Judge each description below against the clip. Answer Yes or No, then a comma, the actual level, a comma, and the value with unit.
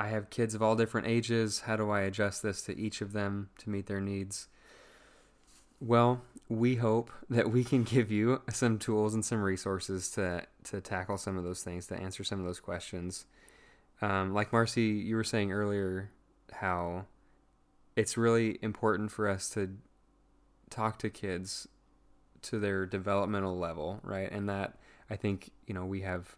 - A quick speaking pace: No, average, 175 wpm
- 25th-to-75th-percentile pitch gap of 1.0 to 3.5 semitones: Yes, narrow, 2.6 semitones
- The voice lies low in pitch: Yes, low, 100 Hz